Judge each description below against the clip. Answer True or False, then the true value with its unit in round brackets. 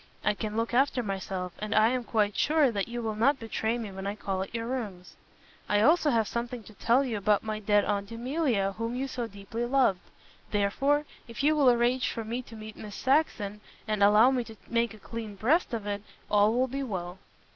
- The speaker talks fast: True (220 wpm)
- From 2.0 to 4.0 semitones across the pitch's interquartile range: True (3.2 semitones)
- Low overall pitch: False (225 Hz)